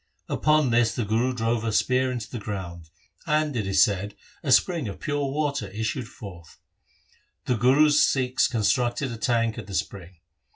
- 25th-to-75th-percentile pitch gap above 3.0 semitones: Yes, average, 4.2 semitones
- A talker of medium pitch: No, low, 120 Hz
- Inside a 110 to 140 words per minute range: No, average, 170 wpm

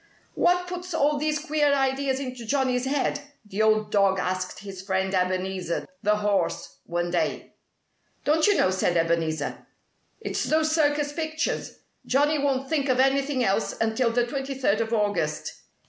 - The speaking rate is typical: Yes, average, 155 wpm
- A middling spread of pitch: No, wide, 7.1 semitones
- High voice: Yes, very high, 250 Hz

